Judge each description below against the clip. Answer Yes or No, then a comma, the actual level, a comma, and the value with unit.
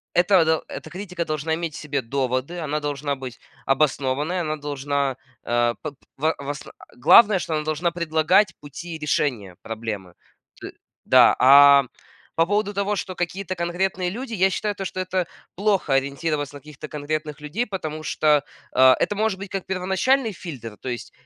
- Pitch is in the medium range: Yes, medium, 155 Hz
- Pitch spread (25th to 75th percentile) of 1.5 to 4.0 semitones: No, average, 4.8 semitones